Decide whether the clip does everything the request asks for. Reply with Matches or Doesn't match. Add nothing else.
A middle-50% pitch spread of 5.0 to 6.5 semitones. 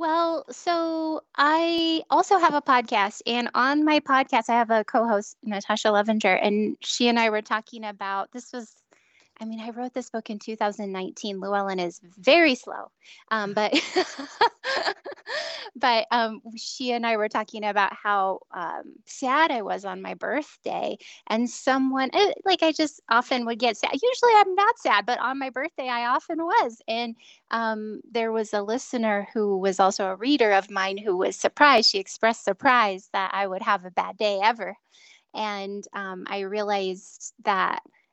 Matches